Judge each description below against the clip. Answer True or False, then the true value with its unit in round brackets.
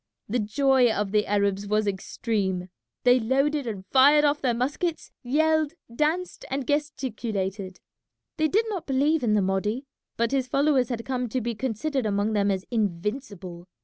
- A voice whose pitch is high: True (245 Hz)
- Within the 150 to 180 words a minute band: True (160 wpm)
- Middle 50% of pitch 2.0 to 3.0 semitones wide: False (5.5 semitones)